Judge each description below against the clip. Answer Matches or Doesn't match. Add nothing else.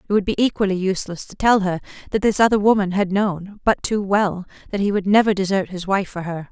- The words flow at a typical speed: Doesn't match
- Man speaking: Doesn't match